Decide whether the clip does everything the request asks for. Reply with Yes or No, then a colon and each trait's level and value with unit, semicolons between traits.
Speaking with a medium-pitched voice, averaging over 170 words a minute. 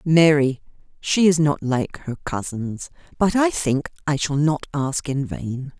No: medium, 145 Hz; average, 165 wpm